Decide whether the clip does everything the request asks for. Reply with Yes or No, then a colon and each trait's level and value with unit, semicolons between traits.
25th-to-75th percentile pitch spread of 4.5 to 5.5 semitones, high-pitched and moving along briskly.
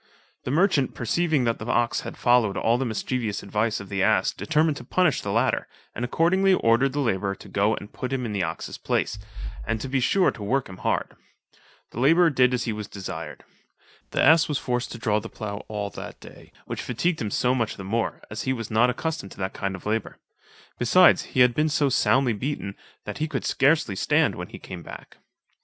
No: average, 4.8 semitones; low, 120 Hz; fast, 220 wpm